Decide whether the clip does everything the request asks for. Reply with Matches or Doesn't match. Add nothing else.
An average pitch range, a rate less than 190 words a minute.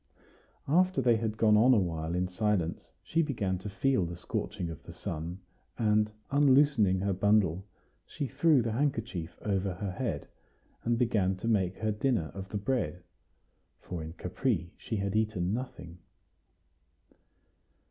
Matches